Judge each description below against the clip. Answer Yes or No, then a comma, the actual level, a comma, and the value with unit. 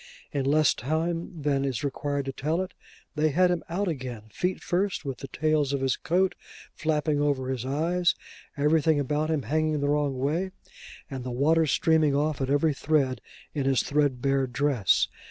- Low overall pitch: No, medium, 145 Hz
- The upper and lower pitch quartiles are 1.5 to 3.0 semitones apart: Yes, average, 2.7 semitones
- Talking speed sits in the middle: Yes, average, 175 wpm